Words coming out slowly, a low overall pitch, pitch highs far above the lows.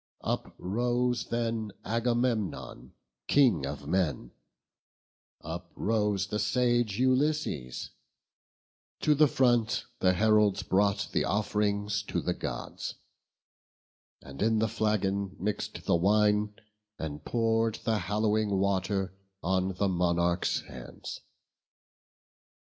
No: slow, 100 wpm; low, 105 Hz; average, 3.5 semitones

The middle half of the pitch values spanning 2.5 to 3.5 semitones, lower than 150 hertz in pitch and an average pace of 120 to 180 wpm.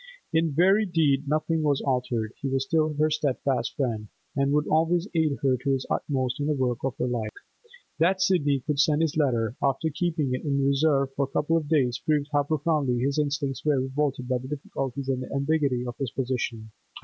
No: average, 2.9 semitones; medium, 140 Hz; fast, 205 wpm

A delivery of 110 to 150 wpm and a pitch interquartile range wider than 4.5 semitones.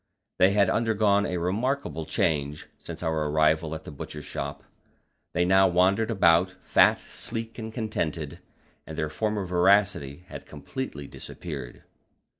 Yes: slow, 135 wpm; average, 5.1 semitones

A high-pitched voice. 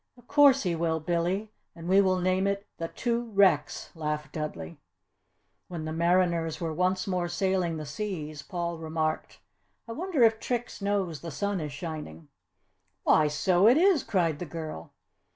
No: medium, 175 Hz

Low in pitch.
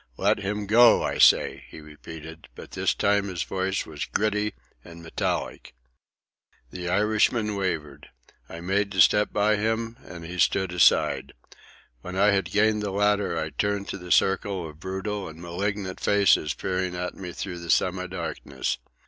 Yes: very low, 95 Hz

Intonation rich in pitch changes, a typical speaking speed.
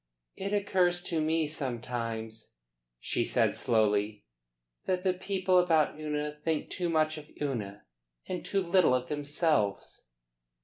No: wide, 6.7 semitones; slow, 130 wpm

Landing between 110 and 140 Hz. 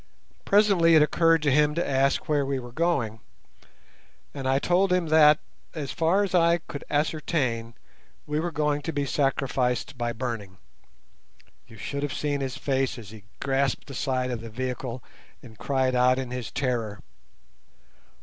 Yes: low, 135 Hz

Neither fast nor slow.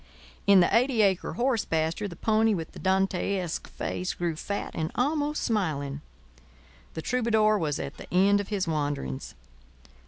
Yes: average, 155 wpm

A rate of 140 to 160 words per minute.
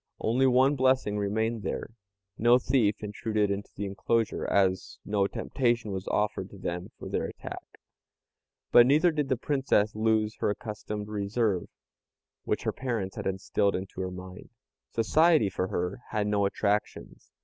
Yes: average, 150 wpm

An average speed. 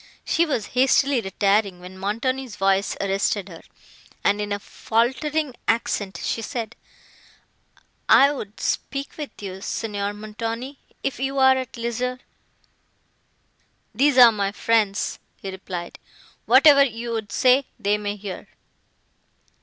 No: slow, 120 wpm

